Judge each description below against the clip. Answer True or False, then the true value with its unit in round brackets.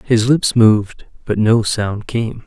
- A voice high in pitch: False (115 Hz)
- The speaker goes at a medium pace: True (170 wpm)